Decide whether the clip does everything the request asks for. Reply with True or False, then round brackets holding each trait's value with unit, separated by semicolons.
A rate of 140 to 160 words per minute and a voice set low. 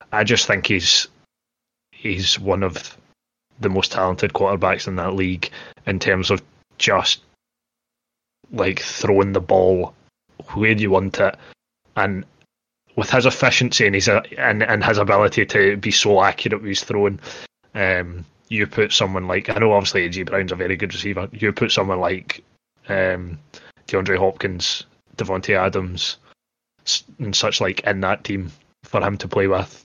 True (155 wpm; 95 Hz)